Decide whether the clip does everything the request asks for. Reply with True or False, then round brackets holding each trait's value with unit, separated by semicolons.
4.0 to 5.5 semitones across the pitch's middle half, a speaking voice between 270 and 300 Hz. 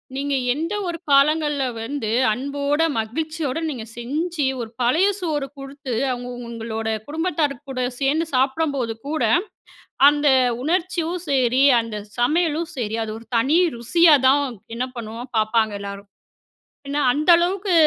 True (4.9 semitones; 280 Hz)